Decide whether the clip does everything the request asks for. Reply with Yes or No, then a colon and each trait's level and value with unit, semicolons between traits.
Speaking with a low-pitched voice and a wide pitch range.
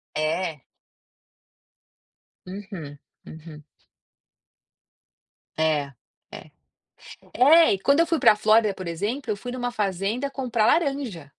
No: high, 210 Hz; wide, 7.2 semitones